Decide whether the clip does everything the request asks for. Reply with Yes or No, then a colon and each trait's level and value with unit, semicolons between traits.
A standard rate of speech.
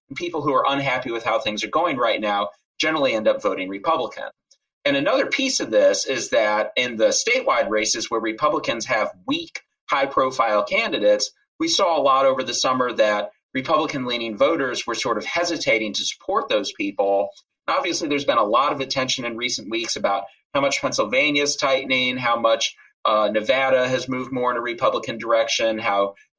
Yes: average, 185 wpm